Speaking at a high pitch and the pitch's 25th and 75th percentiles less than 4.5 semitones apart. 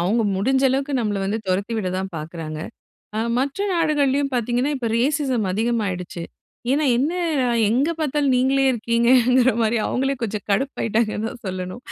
No: high, 235 Hz; average, 4.9 semitones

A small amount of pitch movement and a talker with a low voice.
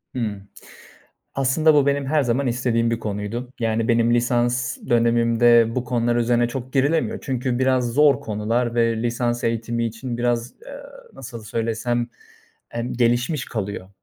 Yes: narrow, 1.5 semitones; low, 120 Hz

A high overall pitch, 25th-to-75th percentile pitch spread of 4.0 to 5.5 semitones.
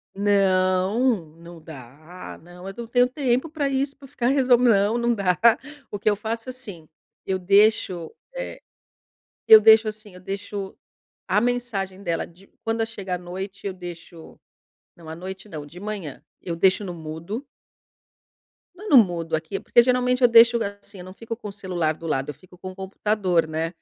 Yes: high, 195 Hz; average, 4.5 semitones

